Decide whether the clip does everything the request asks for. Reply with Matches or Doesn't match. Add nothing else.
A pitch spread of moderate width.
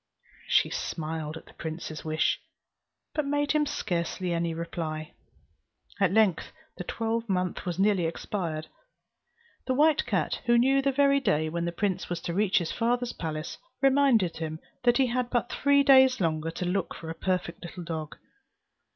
Doesn't match